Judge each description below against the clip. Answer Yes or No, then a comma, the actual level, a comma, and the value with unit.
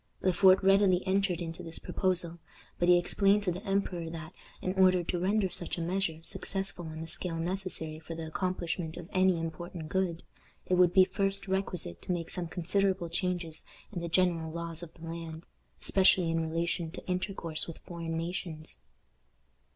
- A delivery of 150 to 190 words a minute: Yes, average, 175 wpm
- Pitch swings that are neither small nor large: No, narrow, 2.2 semitones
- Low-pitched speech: No, medium, 175 Hz